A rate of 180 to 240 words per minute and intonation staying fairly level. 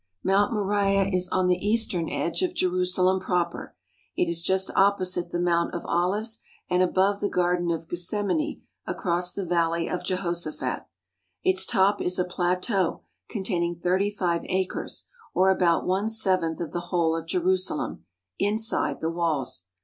No: average, 155 wpm; narrow, 2.2 semitones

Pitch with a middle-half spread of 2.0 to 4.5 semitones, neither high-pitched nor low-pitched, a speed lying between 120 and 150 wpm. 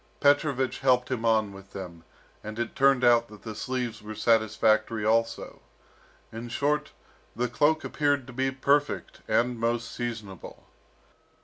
No: average, 3.3 semitones; low, 120 Hz; average, 140 wpm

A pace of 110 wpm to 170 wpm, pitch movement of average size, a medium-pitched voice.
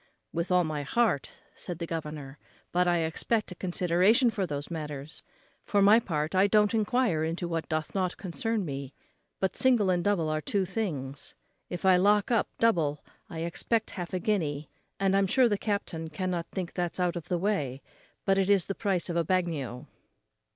No: average, 185 wpm; average, 4.0 semitones; medium, 180 Hz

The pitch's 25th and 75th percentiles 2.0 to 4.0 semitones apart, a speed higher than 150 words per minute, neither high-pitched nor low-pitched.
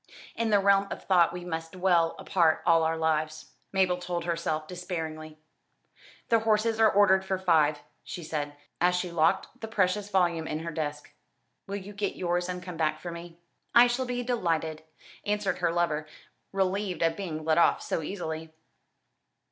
Yes: average, 3.3 semitones; average, 170 wpm; medium, 175 Hz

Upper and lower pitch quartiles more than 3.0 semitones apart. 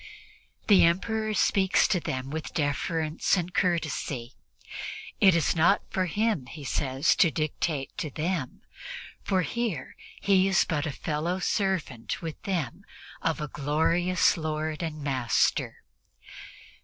Yes: average, 4.0 semitones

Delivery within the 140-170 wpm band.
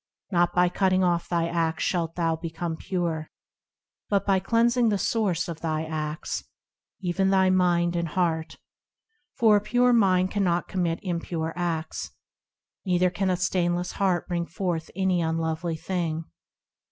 Yes: average, 145 wpm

